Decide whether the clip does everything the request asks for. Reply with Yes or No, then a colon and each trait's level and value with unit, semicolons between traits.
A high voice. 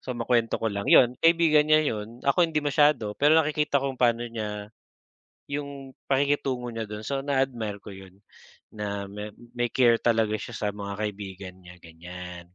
No: low, 115 Hz